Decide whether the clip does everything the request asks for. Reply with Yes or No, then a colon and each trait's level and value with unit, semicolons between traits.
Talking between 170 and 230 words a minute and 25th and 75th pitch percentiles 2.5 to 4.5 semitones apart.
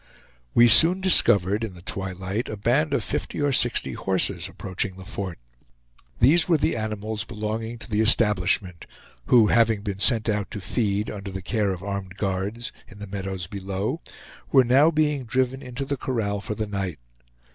Yes: average, 175 wpm; average, 3.8 semitones